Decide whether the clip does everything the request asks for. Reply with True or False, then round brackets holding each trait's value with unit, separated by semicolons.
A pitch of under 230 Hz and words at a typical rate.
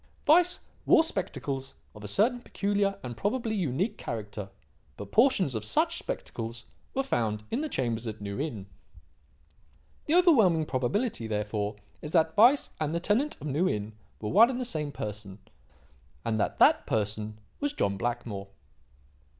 True (140 Hz; 155 wpm)